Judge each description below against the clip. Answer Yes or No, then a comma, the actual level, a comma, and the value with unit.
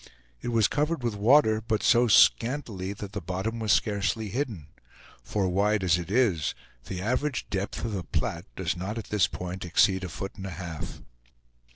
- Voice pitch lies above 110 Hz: No, low, 100 Hz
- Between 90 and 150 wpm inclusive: No, average, 185 wpm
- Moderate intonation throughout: Yes, average, 3.7 semitones